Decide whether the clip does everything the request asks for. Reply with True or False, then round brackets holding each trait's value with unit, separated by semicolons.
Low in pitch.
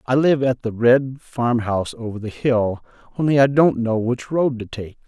True (125 Hz)